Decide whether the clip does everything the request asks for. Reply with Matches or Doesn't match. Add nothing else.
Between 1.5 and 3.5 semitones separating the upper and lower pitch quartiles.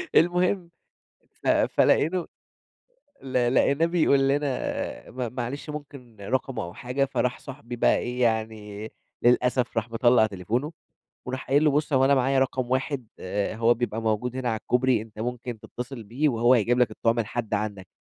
Matches